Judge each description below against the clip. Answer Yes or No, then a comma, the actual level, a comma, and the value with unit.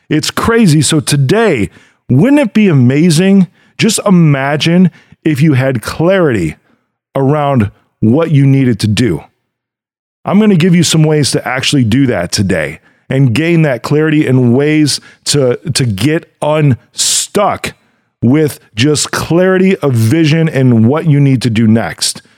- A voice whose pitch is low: No, medium, 145 Hz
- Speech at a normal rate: Yes, average, 145 wpm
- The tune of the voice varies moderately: Yes, average, 4.1 semitones